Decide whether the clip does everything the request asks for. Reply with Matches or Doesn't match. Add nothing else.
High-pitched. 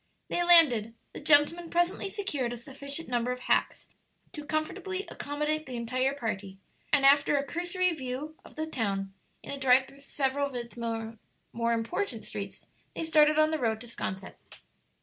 Matches